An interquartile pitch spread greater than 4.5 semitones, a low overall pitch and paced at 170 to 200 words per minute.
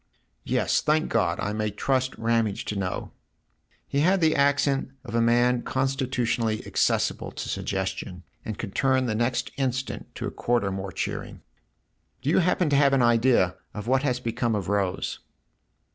No: average, 3.9 semitones; low, 120 Hz; average, 175 wpm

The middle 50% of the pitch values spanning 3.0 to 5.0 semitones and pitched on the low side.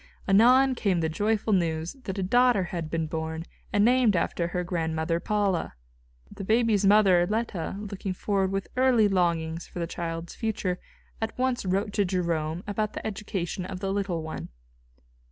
No: average, 3.9 semitones; high, 190 Hz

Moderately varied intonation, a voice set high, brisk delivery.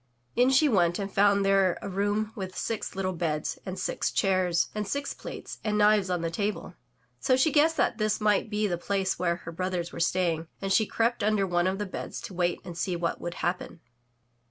Yes: average, 3.2 semitones; high, 195 Hz; fast, 215 wpm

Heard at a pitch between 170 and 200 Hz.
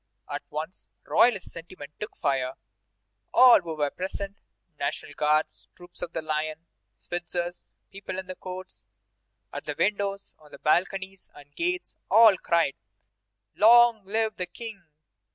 Yes: medium, 185 Hz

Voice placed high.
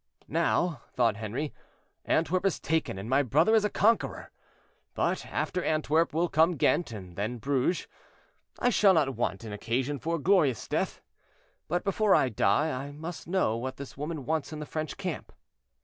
No: medium, 150 Hz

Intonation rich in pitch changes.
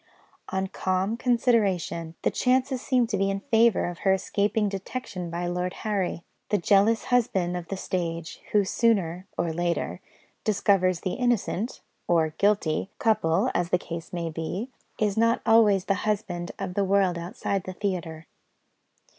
No: average, 3.5 semitones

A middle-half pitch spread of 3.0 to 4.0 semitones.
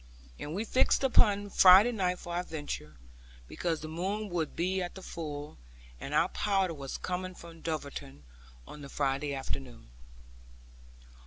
No: average, 4.4 semitones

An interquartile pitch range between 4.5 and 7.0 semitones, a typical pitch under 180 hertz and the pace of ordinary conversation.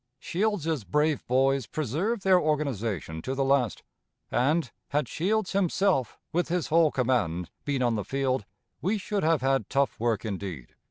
Yes: wide, 5.5 semitones; medium, 140 Hz; average, 155 wpm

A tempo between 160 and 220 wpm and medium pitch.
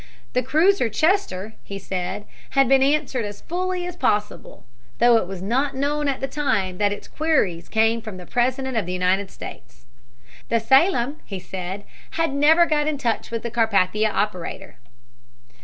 No: average, 170 wpm; high, 235 Hz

